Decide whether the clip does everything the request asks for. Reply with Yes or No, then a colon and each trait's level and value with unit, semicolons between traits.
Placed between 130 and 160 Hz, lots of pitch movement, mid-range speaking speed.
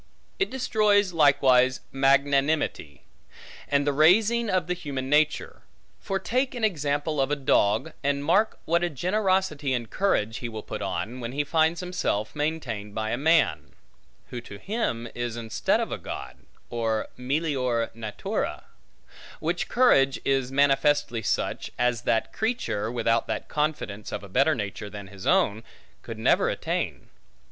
Yes: medium, 140 Hz; wide, 6.1 semitones; average, 150 wpm